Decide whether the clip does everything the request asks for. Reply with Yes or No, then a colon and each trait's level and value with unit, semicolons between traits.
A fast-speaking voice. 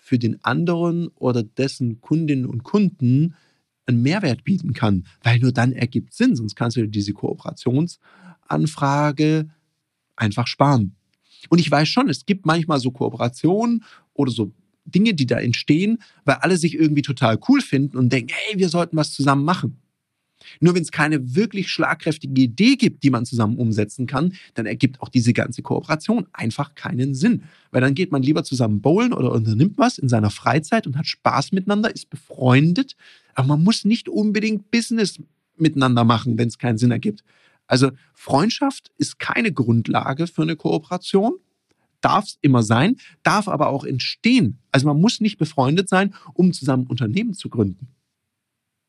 No: average, 165 wpm